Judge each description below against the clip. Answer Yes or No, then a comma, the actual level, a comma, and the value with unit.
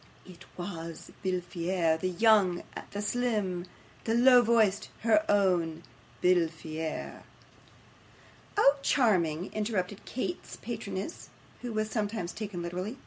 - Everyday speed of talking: No, slow, 110 wpm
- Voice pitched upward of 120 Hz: Yes, high, 190 Hz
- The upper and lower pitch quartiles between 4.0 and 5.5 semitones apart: Yes, average, 4.3 semitones